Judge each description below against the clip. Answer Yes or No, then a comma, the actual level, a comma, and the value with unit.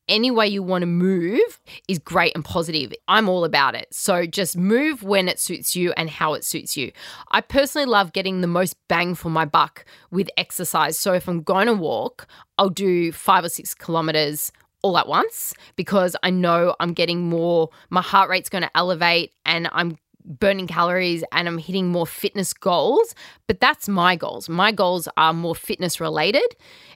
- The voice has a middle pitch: Yes, medium, 180 Hz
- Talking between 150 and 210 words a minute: Yes, average, 190 wpm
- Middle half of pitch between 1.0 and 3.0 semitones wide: Yes, narrow, 2.5 semitones